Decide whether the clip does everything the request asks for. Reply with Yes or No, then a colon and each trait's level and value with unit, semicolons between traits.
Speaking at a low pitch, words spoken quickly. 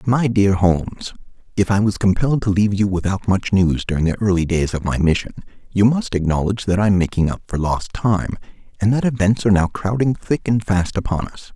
Yes: low, 100 Hz; fast, 220 wpm